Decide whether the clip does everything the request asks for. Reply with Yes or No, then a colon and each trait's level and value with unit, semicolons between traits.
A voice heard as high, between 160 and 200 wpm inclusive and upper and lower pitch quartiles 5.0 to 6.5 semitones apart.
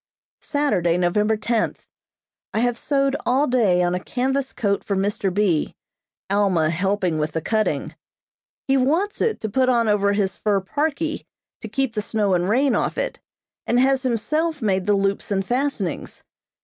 Yes: high, 215 Hz; average, 165 wpm; wide, 5.6 semitones